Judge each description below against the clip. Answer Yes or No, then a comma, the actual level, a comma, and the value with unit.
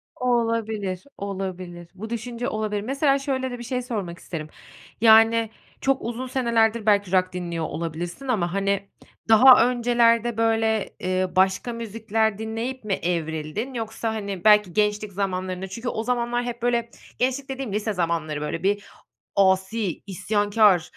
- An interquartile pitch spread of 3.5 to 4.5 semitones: Yes, average, 3.9 semitones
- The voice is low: No, high, 215 Hz